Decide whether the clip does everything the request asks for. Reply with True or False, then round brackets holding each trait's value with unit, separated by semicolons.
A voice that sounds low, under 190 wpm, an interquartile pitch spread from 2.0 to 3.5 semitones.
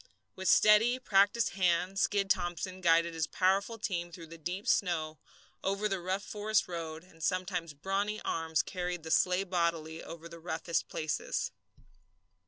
False (180 Hz; 150 wpm; 2.8 semitones)